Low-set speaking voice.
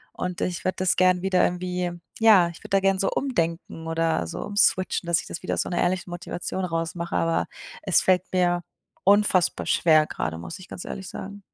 No: medium, 180 Hz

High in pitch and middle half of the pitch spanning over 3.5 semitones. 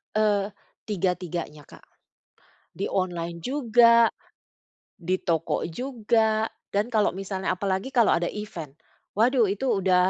Yes: high, 200 Hz; average, 3.9 semitones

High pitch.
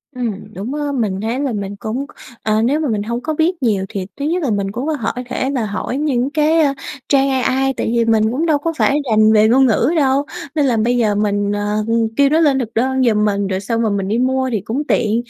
Yes: high, 235 Hz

